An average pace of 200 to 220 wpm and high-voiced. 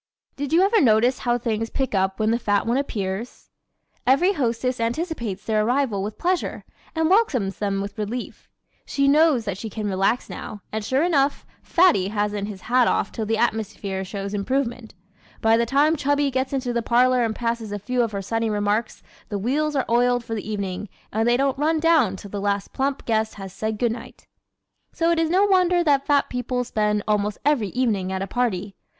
Yes: fast, 205 wpm; high, 235 Hz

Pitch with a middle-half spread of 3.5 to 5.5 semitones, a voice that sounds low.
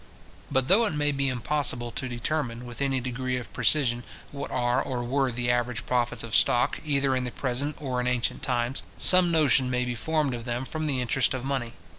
No: narrow, 2.5 semitones; low, 125 Hz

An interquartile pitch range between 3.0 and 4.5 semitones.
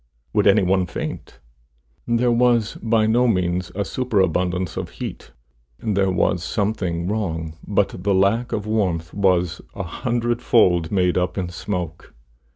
Yes: average, 3.7 semitones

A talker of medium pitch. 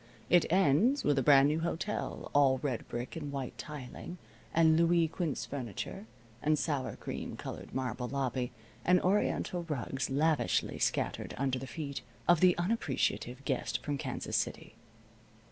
Yes: medium, 145 Hz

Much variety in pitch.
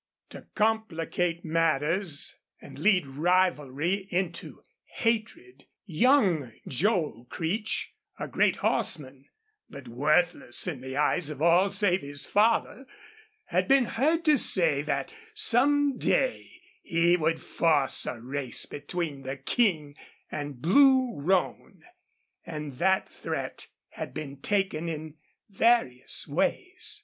Yes: wide, 6.5 semitones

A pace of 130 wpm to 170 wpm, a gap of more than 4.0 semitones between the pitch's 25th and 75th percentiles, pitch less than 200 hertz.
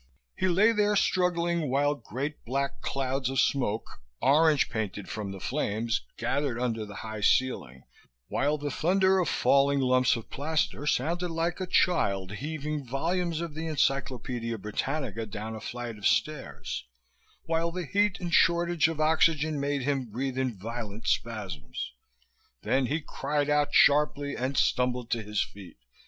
Yes: average, 150 wpm; wide, 5.5 semitones; medium, 140 Hz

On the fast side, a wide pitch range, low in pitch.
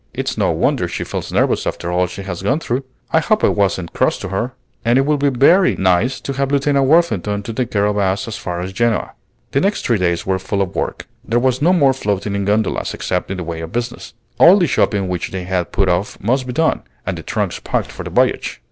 Yes: fast, 245 wpm; wide, 6.2 semitones; low, 105 Hz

